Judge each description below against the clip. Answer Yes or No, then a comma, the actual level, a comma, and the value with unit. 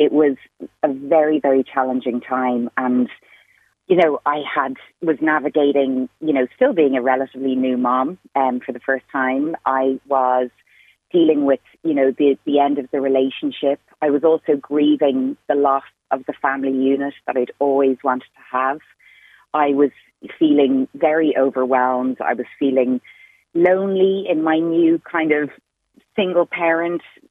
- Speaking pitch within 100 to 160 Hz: Yes, medium, 140 Hz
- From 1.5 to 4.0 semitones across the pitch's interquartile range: Yes, average, 2.9 semitones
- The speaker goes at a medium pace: Yes, average, 160 wpm